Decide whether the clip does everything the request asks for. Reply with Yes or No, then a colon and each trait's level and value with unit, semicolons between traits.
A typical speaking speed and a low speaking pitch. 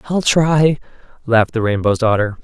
Yes: average, 150 wpm; low, 125 Hz